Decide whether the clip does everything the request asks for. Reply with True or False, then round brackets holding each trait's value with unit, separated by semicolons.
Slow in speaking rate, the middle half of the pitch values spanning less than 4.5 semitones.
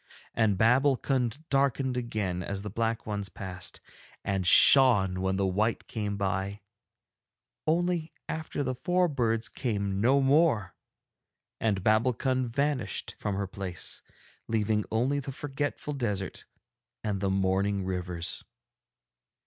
False (120 wpm; 5.4 semitones)